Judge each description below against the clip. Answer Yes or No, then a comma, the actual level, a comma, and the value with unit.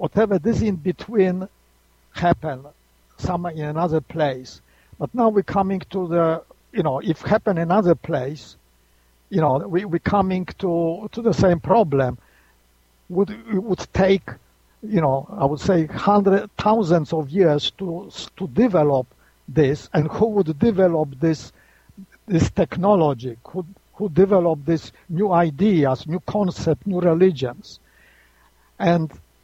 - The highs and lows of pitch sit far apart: Yes, wide, 6.1 semitones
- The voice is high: No, medium, 170 Hz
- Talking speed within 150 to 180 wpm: No, slow, 135 wpm